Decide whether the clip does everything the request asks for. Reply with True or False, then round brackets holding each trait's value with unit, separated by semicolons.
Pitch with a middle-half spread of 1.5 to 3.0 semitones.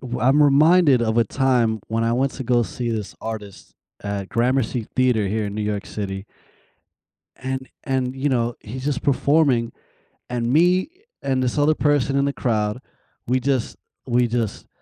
False (3.4 semitones)